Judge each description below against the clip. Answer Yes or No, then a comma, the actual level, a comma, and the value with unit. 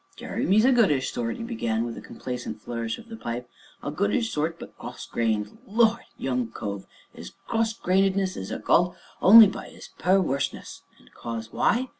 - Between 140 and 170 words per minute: No, average, 190 wpm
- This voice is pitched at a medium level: Yes, medium, 155 Hz